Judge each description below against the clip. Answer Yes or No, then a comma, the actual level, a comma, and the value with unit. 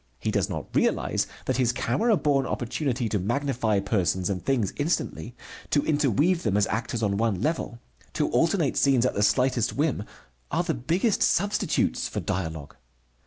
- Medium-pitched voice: No, low, 125 Hz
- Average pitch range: No, wide, 5.8 semitones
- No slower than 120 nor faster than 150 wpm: No, average, 165 wpm